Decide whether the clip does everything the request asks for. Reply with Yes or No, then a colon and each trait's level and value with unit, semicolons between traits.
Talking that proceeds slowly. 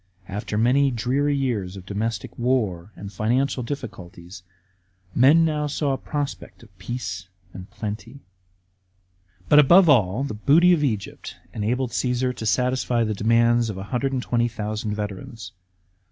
Yes: slow, 130 wpm